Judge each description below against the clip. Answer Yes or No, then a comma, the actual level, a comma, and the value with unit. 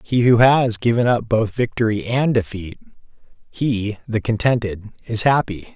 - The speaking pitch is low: Yes, low, 115 Hz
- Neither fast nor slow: Yes, average, 145 wpm